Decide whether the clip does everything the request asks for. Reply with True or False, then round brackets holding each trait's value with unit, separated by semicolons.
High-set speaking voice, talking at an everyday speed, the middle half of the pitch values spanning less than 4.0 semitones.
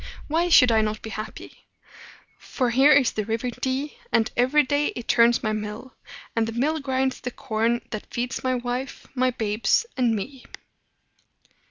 True (245 Hz; 170 wpm; 2.9 semitones)